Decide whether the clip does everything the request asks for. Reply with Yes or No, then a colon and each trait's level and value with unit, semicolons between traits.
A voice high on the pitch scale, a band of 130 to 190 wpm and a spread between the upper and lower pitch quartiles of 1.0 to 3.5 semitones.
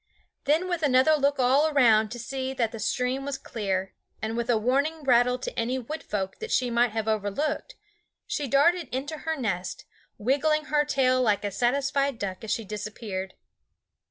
No: very high, 255 Hz; average, 180 wpm; average, 4.4 semitones